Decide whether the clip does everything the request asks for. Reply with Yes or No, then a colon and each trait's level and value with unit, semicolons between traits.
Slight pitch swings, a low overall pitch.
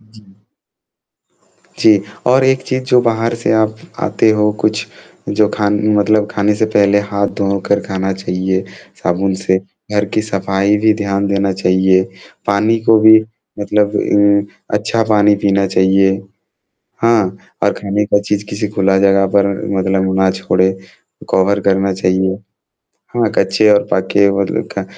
Yes: narrow, 1.8 semitones; low, 100 Hz